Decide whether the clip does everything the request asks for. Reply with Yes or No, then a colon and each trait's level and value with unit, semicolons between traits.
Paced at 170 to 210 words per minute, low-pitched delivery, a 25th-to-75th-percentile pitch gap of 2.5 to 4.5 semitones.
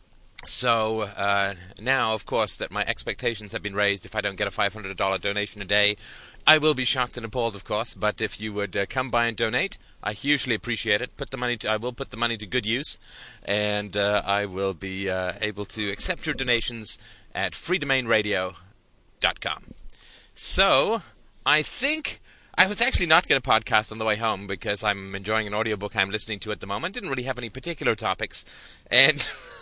Yes: average, 200 wpm; low, 105 Hz; average, 2.9 semitones